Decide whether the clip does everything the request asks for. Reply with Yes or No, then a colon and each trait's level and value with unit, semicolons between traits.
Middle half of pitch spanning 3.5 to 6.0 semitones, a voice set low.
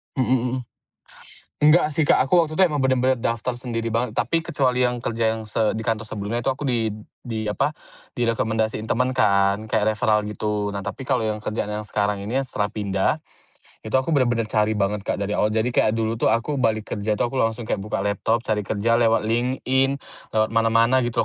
No: average, 3.0 semitones; low, 115 Hz